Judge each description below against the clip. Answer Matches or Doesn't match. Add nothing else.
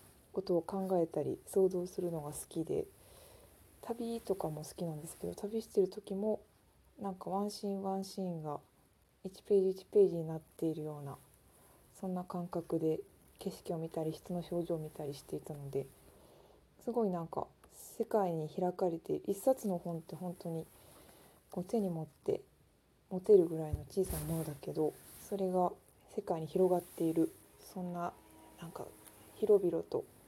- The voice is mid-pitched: Matches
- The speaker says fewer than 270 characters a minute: Doesn't match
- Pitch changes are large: Doesn't match